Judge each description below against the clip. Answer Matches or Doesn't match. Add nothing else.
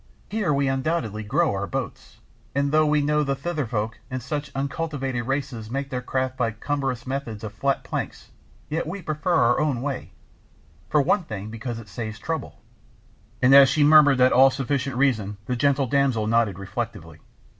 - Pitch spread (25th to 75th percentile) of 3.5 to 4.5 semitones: Matches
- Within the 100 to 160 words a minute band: Doesn't match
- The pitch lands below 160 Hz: Matches